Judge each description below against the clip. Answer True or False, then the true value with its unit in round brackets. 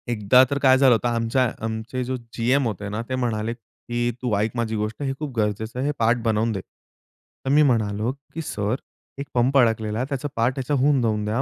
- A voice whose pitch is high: False (120 Hz)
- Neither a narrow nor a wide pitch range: True (3.0 semitones)